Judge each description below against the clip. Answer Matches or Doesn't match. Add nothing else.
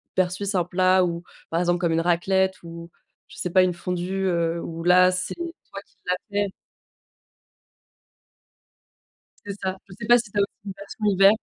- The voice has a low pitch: Doesn't match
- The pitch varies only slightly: Matches